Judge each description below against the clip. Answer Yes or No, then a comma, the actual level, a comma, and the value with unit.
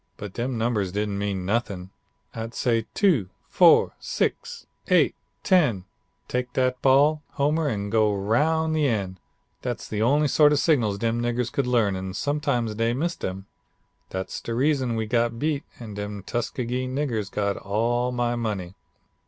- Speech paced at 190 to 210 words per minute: No, average, 160 wpm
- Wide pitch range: No, average, 4.5 semitones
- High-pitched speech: No, low, 120 Hz